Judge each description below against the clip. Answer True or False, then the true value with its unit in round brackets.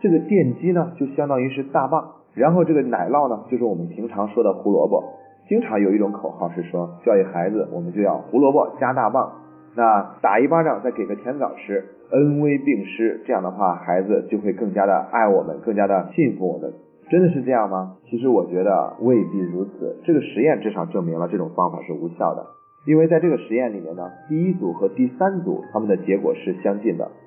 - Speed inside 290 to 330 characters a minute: True (325 characters per minute)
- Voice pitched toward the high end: False (135 Hz)